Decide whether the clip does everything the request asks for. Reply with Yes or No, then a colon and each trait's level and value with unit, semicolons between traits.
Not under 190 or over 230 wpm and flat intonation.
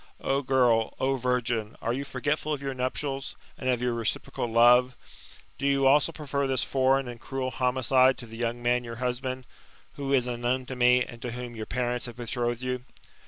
Yes: average, 200 wpm; narrow, 1.7 semitones